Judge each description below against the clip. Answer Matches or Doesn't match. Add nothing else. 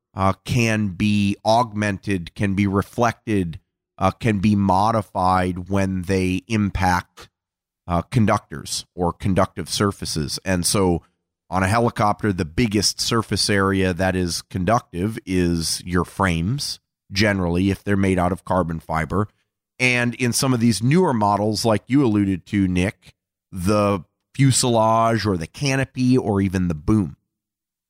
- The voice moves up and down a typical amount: Matches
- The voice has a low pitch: Matches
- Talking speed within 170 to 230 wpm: Doesn't match